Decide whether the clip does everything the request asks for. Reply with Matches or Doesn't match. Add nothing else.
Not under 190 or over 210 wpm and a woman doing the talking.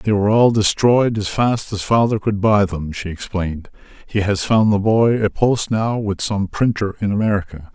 Doesn't match